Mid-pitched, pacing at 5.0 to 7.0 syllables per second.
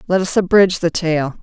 Yes: medium, 175 Hz; 5.6 syllables/s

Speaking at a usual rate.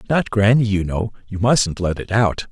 Yes: average, 190 wpm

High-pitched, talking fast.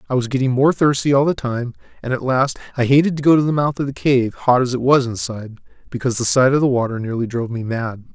No: low, 130 Hz; fast, 265 wpm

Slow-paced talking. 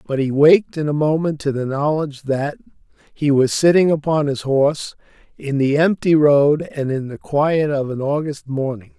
No: average, 185 wpm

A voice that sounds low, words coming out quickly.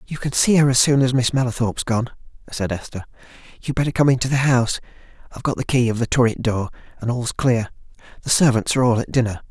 Yes: low, 125 Hz; fast, 210 wpm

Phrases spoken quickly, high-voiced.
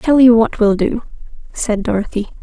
No: average, 175 wpm; high, 225 Hz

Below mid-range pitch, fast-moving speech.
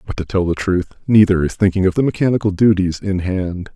Yes: very low, 95 Hz; fast, 225 wpm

